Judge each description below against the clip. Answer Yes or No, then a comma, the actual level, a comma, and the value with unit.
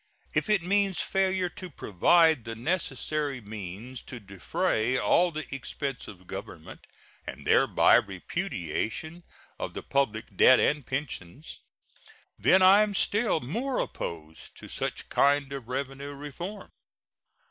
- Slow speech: Yes, slow, 125 wpm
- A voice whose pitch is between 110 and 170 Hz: Yes, medium, 140 Hz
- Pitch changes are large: Yes, wide, 7.6 semitones